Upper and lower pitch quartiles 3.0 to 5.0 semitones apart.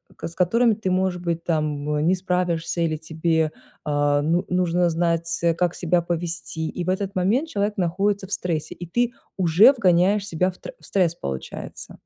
No: narrow, 2.5 semitones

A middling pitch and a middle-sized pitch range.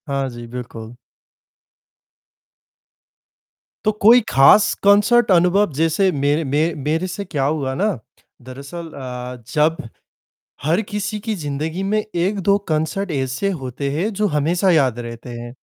No: medium, 155 Hz; wide, 6.6 semitones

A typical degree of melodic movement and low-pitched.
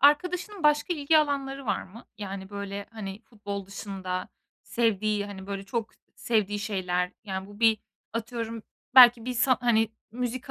No: average, 4.0 semitones; high, 220 Hz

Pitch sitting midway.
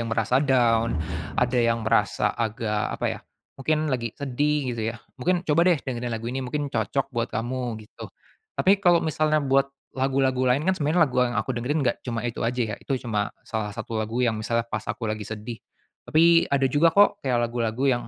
No: low, 125 Hz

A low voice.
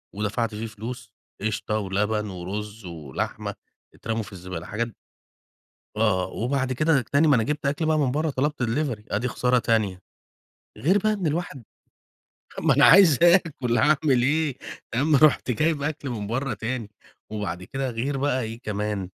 Yes: low, 120 Hz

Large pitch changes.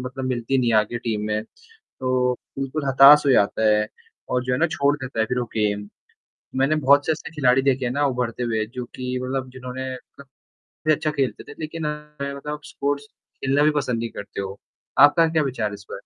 No: average, 3.0 semitones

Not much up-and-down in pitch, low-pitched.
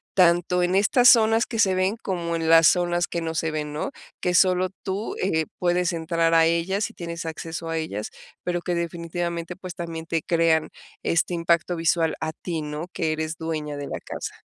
No: narrow, 1.7 semitones; medium, 170 Hz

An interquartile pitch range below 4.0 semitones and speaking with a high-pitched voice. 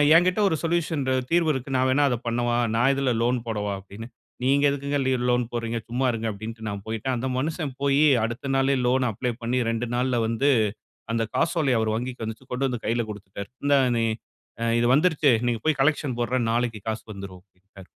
No: average, 3.5 semitones; low, 125 Hz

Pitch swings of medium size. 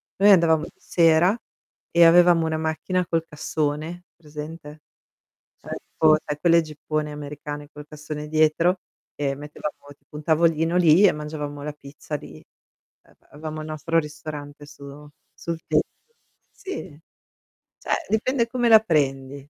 No: narrow, 2.2 semitones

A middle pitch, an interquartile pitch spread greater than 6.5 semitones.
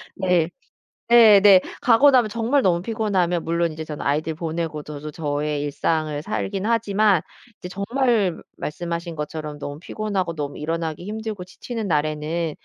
No: medium, 170 Hz; average, 5.3 semitones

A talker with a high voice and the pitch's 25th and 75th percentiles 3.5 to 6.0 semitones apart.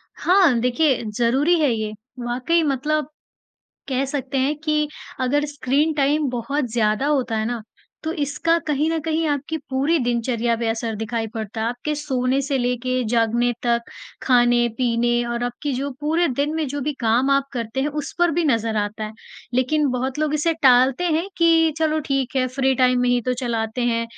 Yes: very high, 260 Hz; average, 3.8 semitones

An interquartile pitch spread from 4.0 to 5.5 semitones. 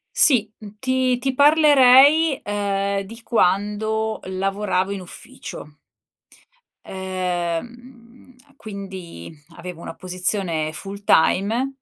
Yes: average, 5.0 semitones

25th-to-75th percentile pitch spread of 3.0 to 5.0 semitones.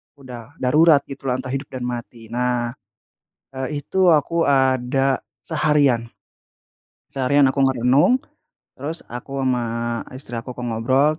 No: narrow, 2.6 semitones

